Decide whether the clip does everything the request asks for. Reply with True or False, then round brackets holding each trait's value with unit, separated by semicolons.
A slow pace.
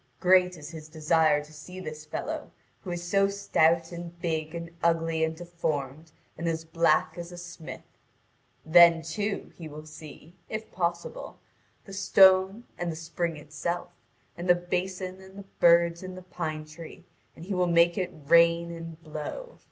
False (165 wpm)